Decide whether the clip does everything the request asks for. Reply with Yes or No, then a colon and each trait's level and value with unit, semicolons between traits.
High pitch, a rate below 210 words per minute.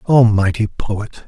No: low, 110 Hz; average, 140 wpm